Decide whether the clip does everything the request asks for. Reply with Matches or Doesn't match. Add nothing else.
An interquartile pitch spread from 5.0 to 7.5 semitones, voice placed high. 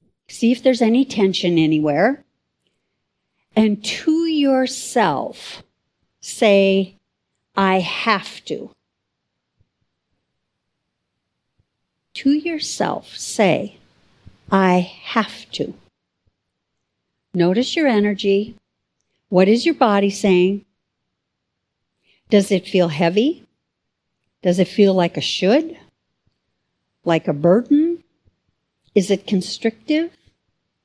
Matches